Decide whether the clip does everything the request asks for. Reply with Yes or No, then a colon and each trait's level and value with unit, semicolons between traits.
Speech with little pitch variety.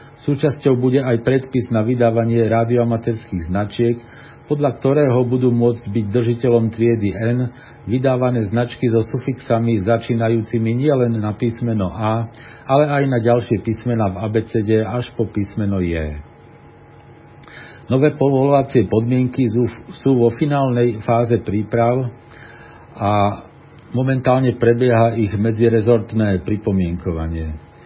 Yes: narrow, 2.1 semitones